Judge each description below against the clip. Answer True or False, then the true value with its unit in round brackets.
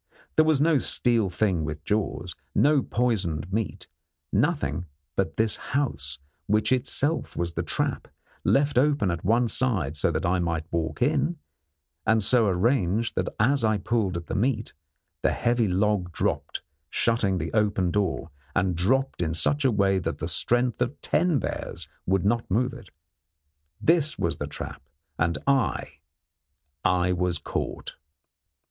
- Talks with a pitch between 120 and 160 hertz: False (105 Hz)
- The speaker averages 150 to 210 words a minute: True (155 wpm)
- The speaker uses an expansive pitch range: True (5.9 semitones)